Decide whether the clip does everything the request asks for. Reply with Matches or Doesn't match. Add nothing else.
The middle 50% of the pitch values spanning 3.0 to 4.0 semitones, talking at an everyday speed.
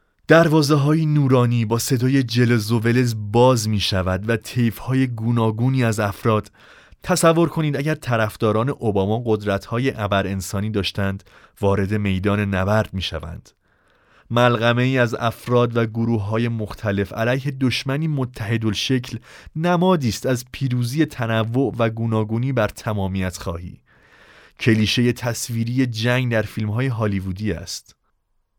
Matches